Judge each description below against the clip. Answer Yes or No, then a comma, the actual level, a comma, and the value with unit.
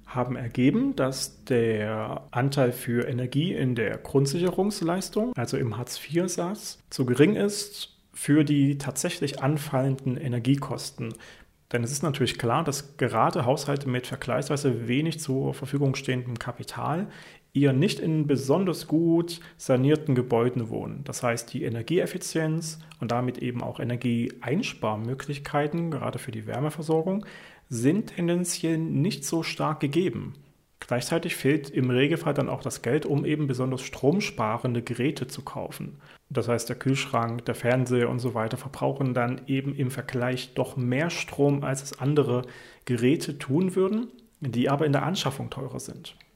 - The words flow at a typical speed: Yes, average, 140 wpm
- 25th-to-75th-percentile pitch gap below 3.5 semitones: No, average, 4.2 semitones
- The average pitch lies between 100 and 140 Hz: Yes, low, 135 Hz